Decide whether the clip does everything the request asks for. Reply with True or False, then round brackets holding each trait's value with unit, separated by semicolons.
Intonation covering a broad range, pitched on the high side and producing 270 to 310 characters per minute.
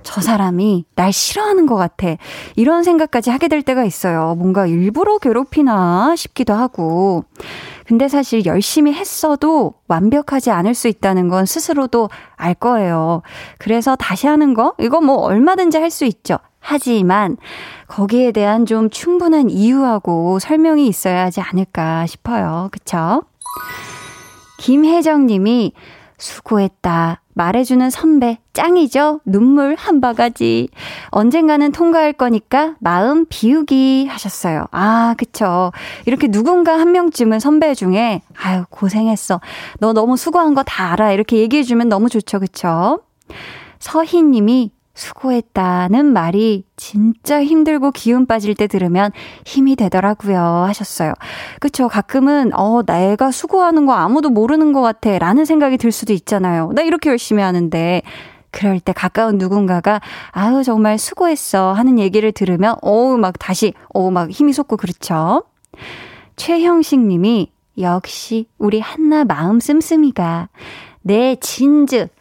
True (6.9 semitones; 225 Hz; 290 characters per minute)